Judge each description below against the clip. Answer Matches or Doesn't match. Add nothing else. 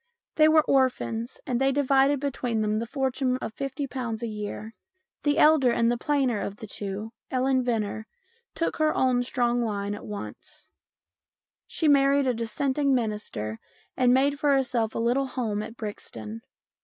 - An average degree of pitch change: Matches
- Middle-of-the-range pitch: Doesn't match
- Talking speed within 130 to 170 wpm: Matches